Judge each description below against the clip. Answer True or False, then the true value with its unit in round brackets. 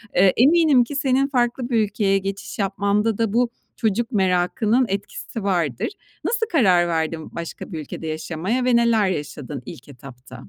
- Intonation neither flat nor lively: False (5.7 semitones)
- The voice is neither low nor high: False (200 Hz)